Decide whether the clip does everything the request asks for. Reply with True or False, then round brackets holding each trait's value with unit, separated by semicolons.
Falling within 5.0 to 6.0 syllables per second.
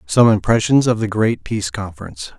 True (5.8 syllables/s)